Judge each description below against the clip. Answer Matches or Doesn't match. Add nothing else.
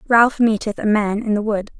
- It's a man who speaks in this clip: Doesn't match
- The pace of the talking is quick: Matches